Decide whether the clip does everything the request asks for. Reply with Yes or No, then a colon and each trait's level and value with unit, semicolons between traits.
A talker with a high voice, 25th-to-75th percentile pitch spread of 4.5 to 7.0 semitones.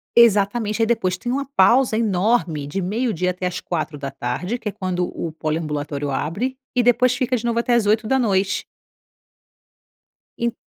Yes: high, 200 Hz; wide, 5.5 semitones